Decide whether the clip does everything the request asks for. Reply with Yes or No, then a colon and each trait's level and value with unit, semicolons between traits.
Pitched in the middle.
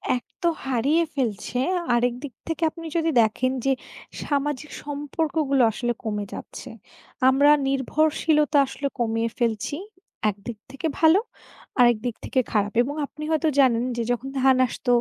No: very high, 270 Hz